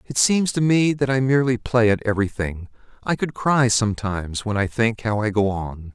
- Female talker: No, male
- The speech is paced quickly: Yes, fast, 210 wpm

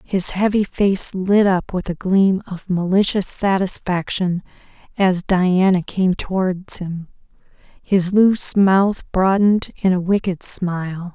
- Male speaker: No, female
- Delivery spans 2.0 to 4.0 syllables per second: Yes, 3.8 syllables/s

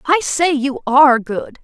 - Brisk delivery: No, average, 185 wpm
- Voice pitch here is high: Yes, very high, 285 Hz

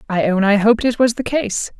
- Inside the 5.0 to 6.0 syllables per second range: Yes, 5.7 syllables/s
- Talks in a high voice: Yes, high, 220 Hz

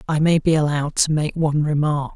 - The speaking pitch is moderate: Yes, medium, 150 Hz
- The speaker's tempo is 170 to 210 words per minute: No, fast, 225 wpm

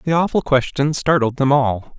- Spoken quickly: No, average, 180 wpm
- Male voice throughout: Yes, male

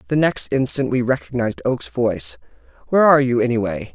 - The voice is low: Yes, low, 120 Hz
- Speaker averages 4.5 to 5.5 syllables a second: No, 6.6 syllables/s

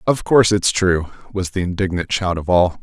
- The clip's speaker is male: Yes, male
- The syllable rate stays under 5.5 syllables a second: Yes, 5.3 syllables/s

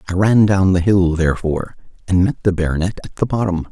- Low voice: Yes, very low, 90 Hz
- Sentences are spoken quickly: Yes, fast, 210 wpm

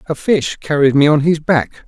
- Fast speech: Yes, fast, 225 wpm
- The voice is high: No, medium, 145 Hz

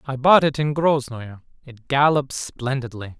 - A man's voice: Yes, male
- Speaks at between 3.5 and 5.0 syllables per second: Yes, 4.2 syllables/s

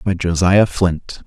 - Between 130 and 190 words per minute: Yes, average, 140 wpm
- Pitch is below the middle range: Yes, very low, 90 Hz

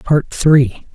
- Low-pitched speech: No, medium, 145 Hz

